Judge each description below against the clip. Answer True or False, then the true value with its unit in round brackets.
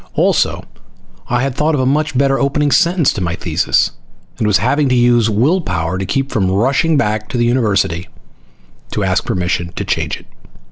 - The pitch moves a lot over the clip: True (6.4 semitones)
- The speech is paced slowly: False (190 wpm)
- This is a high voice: False (120 Hz)